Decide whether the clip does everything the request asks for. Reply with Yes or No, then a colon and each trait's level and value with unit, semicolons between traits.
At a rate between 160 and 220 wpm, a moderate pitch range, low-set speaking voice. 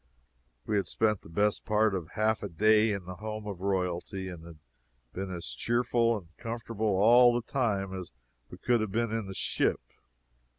Yes: average, 185 wpm; average, 3.2 semitones; low, 105 Hz